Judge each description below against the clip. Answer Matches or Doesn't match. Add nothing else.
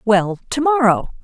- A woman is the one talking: Matches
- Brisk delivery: Doesn't match